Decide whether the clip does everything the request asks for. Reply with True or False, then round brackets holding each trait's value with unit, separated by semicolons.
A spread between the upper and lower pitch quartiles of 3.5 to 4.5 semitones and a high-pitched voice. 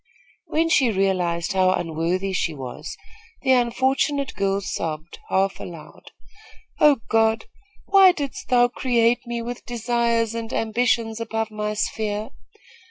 True (4.0 semitones; 225 Hz)